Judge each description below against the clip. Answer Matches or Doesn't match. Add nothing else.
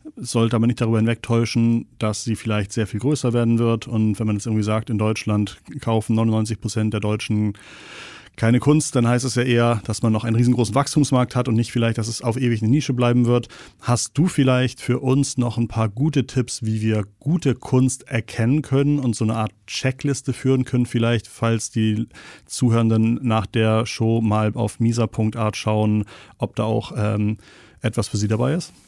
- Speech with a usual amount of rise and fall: Doesn't match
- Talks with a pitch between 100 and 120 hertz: Matches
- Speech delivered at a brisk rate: Matches